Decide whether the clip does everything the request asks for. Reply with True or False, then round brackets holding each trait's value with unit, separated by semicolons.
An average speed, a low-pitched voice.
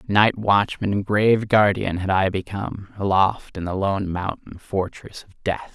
True (165 wpm; 100 Hz)